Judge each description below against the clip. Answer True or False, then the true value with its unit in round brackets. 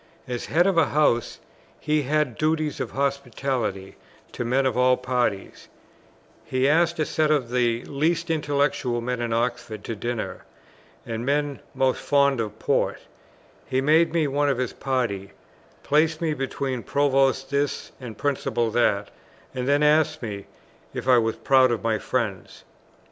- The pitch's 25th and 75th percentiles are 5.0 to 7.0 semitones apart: False (3.6 semitones)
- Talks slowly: False (155 wpm)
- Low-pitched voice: True (130 Hz)